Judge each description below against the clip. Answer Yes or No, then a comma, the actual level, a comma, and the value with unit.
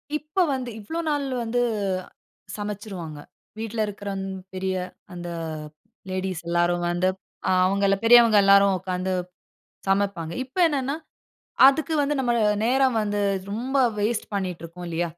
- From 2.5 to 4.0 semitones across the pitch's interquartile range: No, average, 4.7 semitones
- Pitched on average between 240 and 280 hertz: No, high, 200 Hz